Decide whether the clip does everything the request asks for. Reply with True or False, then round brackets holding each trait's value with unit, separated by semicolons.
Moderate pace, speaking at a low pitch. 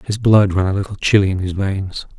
False (245 wpm; 100 Hz)